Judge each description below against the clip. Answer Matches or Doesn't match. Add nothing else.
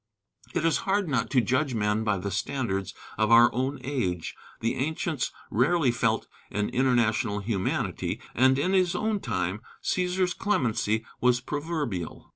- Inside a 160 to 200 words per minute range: Doesn't match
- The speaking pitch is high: Doesn't match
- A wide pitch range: Matches